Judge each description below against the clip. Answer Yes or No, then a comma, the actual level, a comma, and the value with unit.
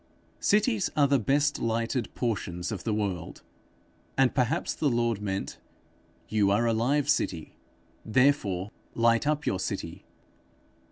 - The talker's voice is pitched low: Yes, low, 115 Hz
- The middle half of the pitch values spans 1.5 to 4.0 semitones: No, average, 5.3 semitones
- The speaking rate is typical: No, slow, 130 wpm